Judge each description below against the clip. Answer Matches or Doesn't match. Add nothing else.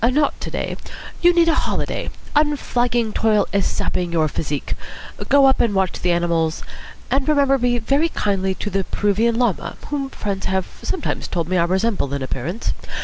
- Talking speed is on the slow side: Doesn't match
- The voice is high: Matches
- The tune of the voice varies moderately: Doesn't match